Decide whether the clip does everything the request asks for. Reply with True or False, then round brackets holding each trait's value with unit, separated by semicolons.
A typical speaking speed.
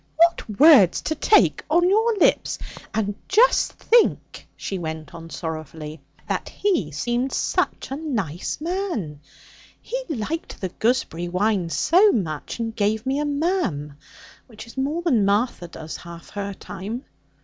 True (145 wpm)